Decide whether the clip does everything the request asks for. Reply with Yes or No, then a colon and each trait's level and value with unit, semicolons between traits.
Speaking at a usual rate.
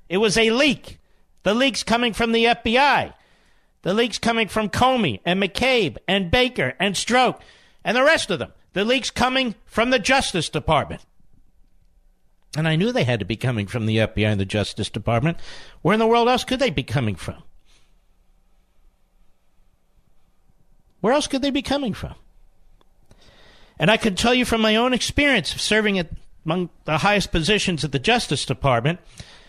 Yes: average, 175 wpm